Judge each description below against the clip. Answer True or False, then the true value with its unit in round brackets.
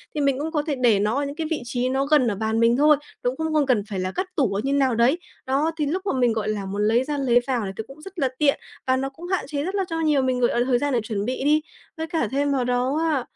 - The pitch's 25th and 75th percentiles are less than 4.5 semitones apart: True (3.9 semitones)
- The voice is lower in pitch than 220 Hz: False (270 Hz)